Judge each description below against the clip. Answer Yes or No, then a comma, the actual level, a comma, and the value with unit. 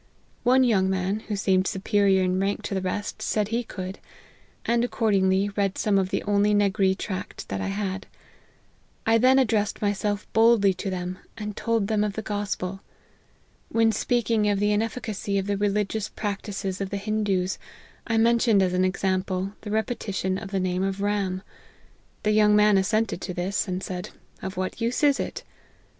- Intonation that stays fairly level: Yes, narrow, 2.2 semitones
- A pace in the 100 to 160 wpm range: No, average, 185 wpm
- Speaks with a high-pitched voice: Yes, high, 200 Hz